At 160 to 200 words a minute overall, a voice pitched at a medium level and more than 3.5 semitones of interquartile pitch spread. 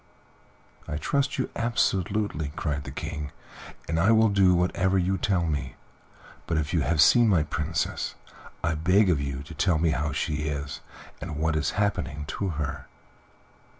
No: average, 165 wpm; very low, 80 Hz; average, 4.4 semitones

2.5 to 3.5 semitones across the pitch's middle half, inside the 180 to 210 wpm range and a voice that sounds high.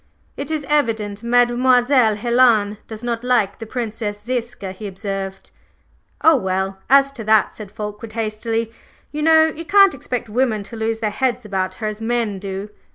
No: average, 3.1 semitones; average, 165 wpm; high, 225 Hz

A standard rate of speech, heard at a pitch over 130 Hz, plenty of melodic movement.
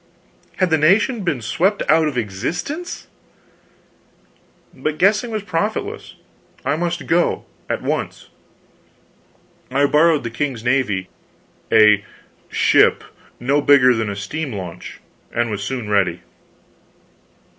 No: slow, 115 wpm; medium, 140 Hz; wide, 7.8 semitones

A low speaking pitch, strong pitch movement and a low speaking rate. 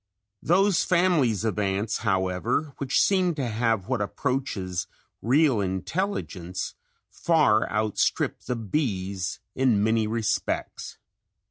Yes: low, 115 Hz; wide, 6.3 semitones; slow, 105 wpm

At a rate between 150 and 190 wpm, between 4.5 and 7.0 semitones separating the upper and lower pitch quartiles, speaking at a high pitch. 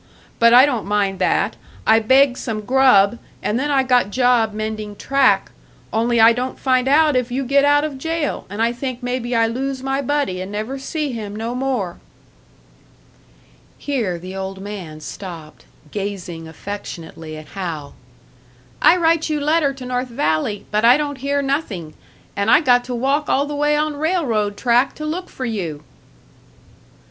Yes: average, 170 wpm; average, 5.2 semitones; high, 245 Hz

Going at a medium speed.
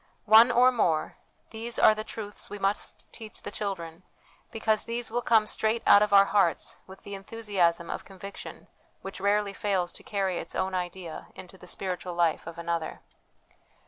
Yes: average, 175 wpm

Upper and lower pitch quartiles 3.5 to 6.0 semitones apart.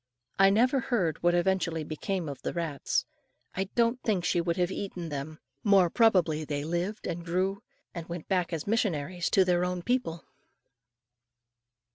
No: average, 2.9 semitones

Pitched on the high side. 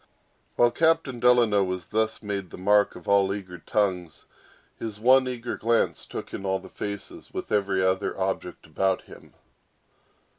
No: low, 100 Hz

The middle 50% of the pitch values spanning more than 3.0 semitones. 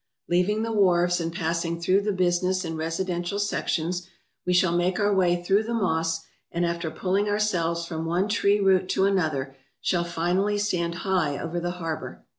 No: narrow, 2.5 semitones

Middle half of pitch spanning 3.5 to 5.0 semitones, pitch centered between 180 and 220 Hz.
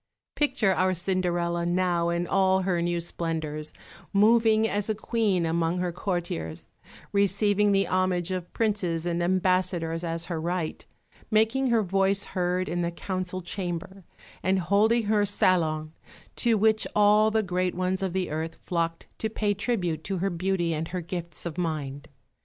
No: average, 2.8 semitones; medium, 185 Hz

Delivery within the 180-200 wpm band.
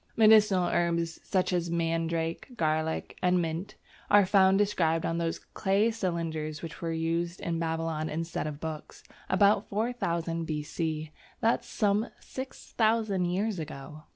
No: slow, 135 wpm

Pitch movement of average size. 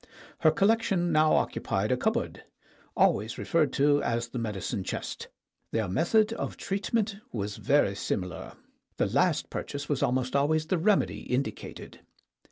No: wide, 7.1 semitones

